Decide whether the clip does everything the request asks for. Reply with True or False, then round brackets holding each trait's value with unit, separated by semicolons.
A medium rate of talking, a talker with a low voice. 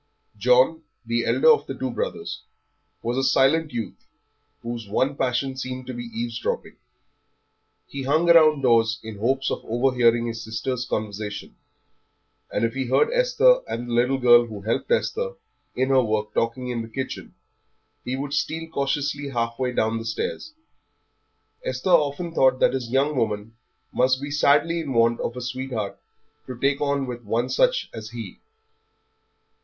True (160 wpm; 130 Hz)